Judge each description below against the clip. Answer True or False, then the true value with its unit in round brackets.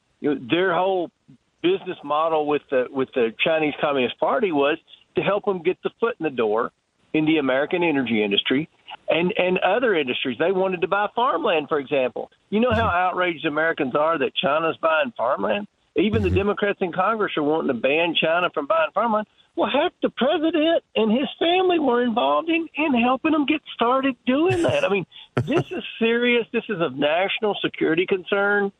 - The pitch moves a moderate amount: False (8.3 semitones)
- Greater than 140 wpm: True (185 wpm)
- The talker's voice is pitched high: True (200 Hz)